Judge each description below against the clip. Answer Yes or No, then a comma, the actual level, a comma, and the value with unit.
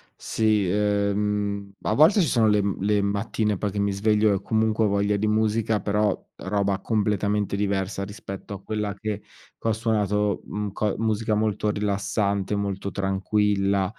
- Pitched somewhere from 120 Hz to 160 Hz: No, low, 105 Hz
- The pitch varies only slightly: Yes, narrow, 1.1 semitones